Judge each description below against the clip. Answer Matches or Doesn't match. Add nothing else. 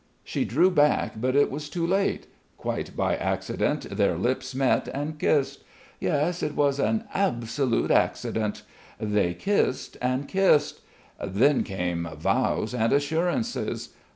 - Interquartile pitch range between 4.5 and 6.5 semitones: Matches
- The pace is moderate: Doesn't match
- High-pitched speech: Doesn't match